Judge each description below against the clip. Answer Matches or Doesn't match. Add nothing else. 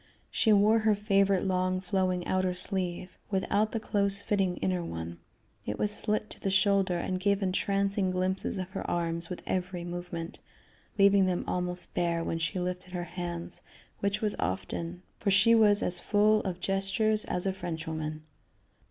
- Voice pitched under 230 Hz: Matches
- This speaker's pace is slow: Doesn't match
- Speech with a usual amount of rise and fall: Doesn't match